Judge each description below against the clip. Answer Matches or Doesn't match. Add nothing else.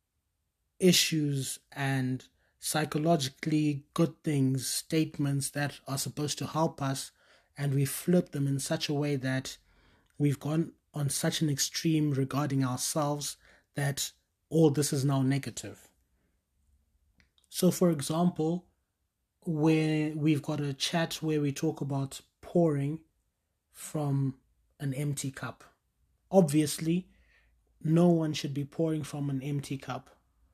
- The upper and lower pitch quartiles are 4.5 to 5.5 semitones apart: Doesn't match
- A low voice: Doesn't match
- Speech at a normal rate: Doesn't match